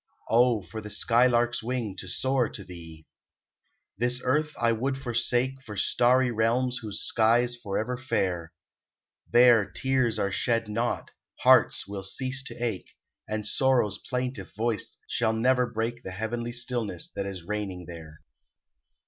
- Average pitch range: Yes, average, 3.5 semitones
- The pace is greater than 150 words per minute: No, average, 145 wpm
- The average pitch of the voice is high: No, low, 115 Hz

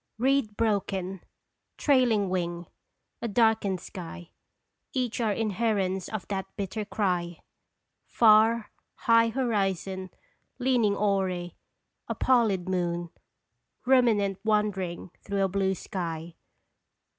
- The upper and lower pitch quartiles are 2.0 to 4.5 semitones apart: Yes, average, 3.3 semitones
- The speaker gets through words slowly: Yes, slow, 100 wpm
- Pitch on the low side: No, high, 200 Hz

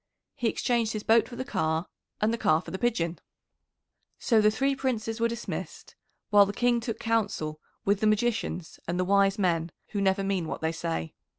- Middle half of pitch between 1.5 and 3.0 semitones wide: No, average, 4.4 semitones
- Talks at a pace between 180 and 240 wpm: Yes, average, 195 wpm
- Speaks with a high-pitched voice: Yes, high, 210 Hz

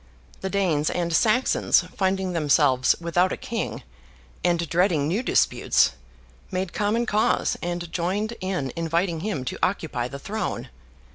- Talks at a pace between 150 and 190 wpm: No, slow, 135 wpm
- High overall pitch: No, medium, 175 Hz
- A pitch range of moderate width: Yes, average, 3.3 semitones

